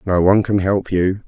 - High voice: No, very low, 95 Hz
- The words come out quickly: Yes, fast, 235 wpm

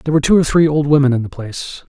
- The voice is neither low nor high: Yes, medium, 145 Hz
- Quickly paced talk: Yes, fast, 305 wpm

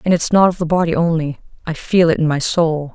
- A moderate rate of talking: No, fast, 265 wpm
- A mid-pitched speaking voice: Yes, medium, 165 Hz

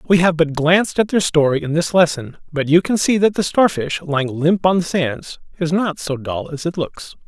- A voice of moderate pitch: Yes, medium, 165 Hz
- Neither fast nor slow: No, fast, 240 wpm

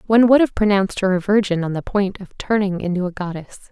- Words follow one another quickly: Yes, fast, 240 wpm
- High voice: Yes, high, 195 Hz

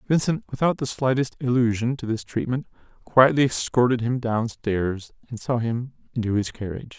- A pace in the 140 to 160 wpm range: Yes, average, 155 wpm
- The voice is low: Yes, low, 120 Hz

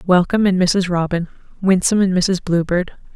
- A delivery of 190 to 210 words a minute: No, average, 150 wpm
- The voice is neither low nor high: Yes, medium, 180 Hz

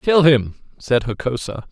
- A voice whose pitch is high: No, low, 135 Hz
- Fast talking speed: No, average, 140 wpm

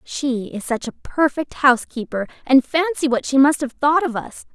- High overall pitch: Yes, very high, 270 Hz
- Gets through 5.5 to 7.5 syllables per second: No, 4.9 syllables/s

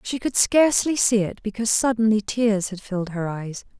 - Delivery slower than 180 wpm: No, average, 190 wpm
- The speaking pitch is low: No, high, 215 Hz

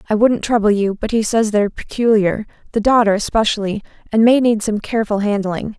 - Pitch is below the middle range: No, high, 215 Hz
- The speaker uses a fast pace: No, average, 165 wpm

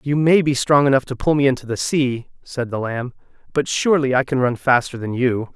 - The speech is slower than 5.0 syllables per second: No, 5.5 syllables/s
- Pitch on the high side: No, low, 135 Hz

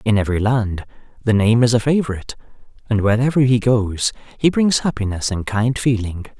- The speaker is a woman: No, male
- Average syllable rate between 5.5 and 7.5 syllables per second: Yes, 5.6 syllables/s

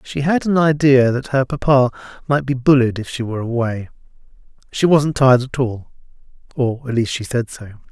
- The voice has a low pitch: Yes, low, 130 Hz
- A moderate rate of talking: Yes, average, 190 wpm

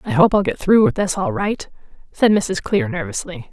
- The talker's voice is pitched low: No, high, 200 Hz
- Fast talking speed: Yes, fast, 220 wpm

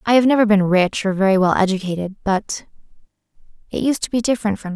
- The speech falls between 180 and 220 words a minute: Yes, average, 200 wpm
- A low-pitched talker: No, high, 205 Hz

